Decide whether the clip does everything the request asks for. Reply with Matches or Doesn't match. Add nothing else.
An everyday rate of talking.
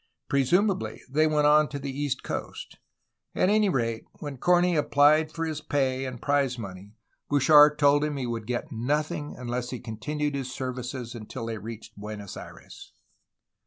Matches